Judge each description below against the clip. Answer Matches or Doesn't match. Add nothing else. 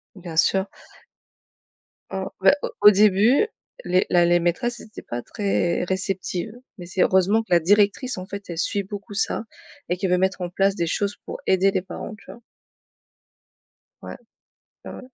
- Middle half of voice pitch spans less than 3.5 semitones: Matches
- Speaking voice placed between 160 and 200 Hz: Matches